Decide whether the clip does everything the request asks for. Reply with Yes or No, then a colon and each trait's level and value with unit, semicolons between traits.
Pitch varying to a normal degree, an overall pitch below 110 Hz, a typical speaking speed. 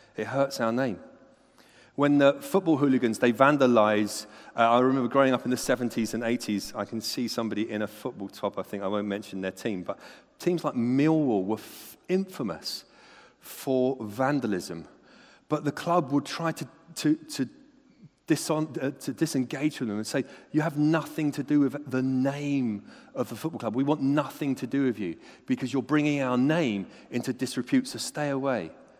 No: average, 4.2 semitones; low, 135 Hz; average, 180 wpm